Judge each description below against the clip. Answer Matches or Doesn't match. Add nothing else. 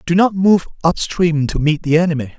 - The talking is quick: Matches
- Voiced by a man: Matches